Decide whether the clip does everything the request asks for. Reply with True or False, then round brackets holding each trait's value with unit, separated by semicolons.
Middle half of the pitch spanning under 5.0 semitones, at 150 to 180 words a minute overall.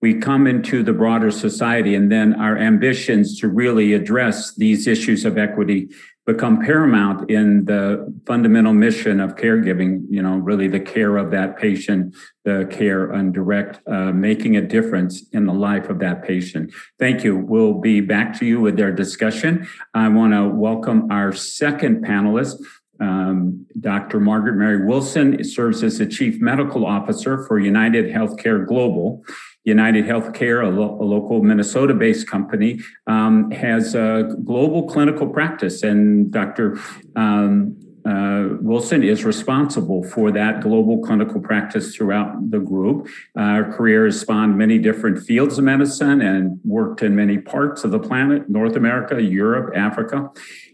False (5.6 semitones; 155 wpm)